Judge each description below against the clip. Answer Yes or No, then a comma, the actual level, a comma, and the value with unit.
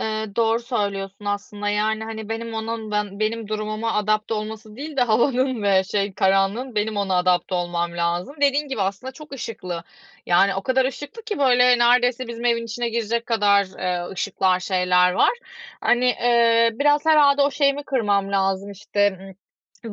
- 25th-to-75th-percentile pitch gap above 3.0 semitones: Yes, average, 3.6 semitones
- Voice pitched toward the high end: Yes, high, 220 Hz